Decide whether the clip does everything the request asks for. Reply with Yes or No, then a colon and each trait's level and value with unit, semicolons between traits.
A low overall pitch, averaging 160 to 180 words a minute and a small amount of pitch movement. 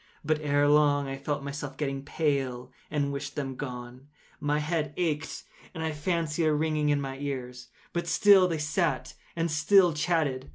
No: medium, 150 Hz; average, 170 wpm; narrow, 2.3 semitones